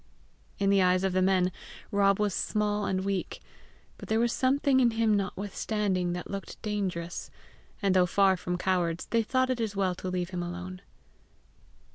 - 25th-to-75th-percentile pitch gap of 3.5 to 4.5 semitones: No, narrow, 2.5 semitones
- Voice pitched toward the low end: No, high, 195 Hz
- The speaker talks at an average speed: Yes, average, 175 wpm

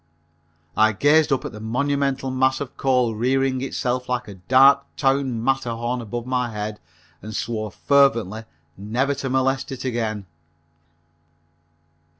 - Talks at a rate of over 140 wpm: No, slow, 135 wpm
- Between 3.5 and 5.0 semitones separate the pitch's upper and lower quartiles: No, average, 3.1 semitones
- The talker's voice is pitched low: Yes, low, 125 Hz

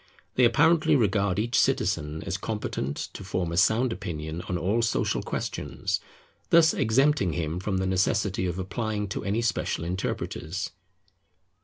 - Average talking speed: Yes, average, 145 wpm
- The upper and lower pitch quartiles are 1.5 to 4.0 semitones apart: No, average, 4.4 semitones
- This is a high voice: No, low, 100 Hz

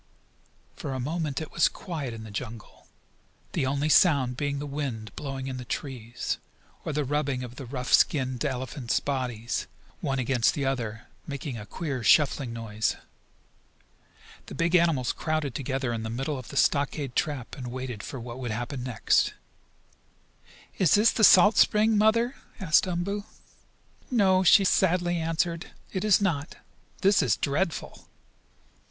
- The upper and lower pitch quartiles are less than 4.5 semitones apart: No, average, 5.1 semitones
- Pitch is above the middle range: No, medium, 140 Hz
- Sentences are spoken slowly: No, average, 155 wpm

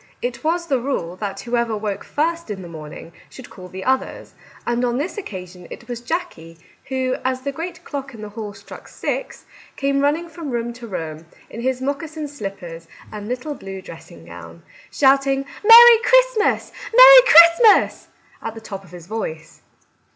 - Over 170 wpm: Yes, average, 180 wpm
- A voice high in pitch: Yes, high, 245 Hz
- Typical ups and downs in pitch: No, wide, 7.5 semitones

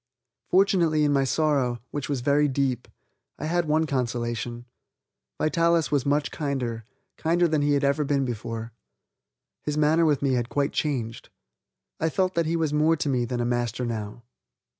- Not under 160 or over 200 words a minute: Yes, average, 170 wpm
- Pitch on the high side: No, medium, 140 Hz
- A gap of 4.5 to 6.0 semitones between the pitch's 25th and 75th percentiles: No, average, 4.1 semitones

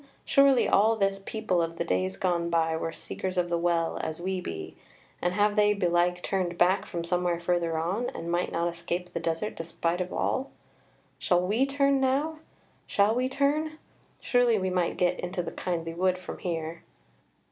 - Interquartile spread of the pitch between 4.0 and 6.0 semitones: No, average, 3.6 semitones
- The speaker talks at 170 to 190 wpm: Yes, average, 180 wpm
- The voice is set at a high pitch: No, medium, 180 Hz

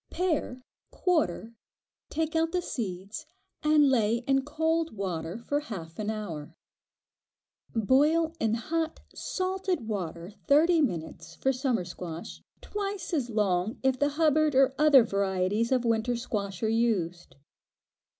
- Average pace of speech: No, slow, 130 wpm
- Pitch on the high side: Yes, high, 240 Hz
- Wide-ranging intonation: Yes, wide, 7.5 semitones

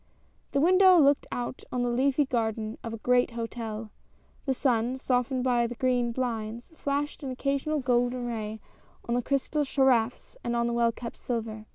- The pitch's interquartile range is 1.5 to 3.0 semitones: Yes, narrow, 2.5 semitones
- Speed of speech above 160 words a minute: Yes, average, 175 wpm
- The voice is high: Yes, high, 245 Hz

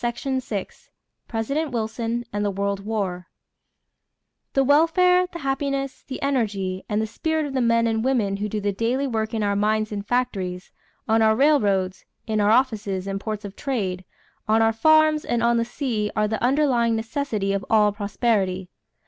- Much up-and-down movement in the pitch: No, average, 4.3 semitones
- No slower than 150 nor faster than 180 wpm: Yes, average, 175 wpm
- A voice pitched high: Yes, high, 225 Hz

